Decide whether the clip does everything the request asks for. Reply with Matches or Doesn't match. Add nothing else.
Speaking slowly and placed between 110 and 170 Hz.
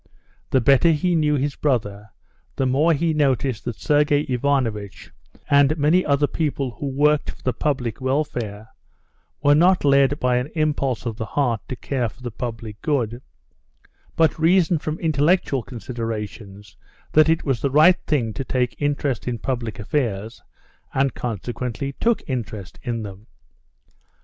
Doesn't match